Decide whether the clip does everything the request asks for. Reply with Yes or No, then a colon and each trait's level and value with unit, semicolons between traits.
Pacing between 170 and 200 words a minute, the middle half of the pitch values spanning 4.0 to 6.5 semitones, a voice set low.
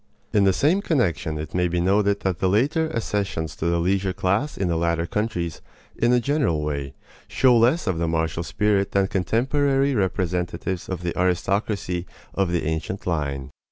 Yes: average, 175 wpm; average, 4.4 semitones; very low, 95 Hz